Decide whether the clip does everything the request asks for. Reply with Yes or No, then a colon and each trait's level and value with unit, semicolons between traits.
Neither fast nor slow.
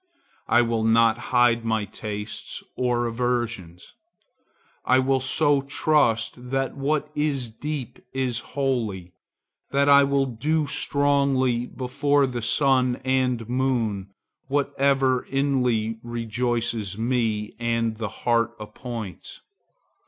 No: slow, 110 wpm